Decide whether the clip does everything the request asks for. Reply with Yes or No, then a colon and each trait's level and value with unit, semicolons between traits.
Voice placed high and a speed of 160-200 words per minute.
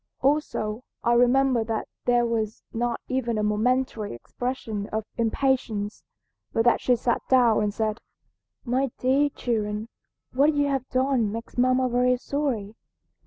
No: high, 240 Hz; average, 140 wpm